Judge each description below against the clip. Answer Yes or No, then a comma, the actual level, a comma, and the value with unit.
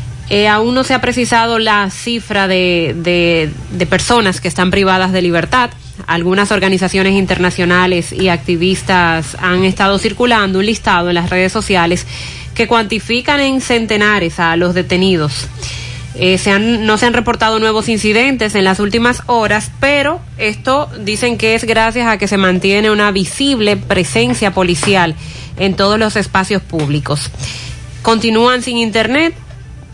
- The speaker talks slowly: No, average, 145 wpm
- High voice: Yes, high, 195 Hz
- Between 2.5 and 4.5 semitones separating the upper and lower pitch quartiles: Yes, average, 4.2 semitones